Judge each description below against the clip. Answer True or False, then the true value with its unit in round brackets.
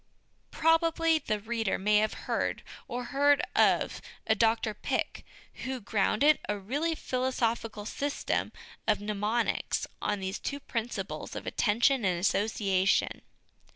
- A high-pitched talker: True (225 Hz)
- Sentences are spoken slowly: True (120 wpm)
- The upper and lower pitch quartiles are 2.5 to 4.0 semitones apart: False (4.7 semitones)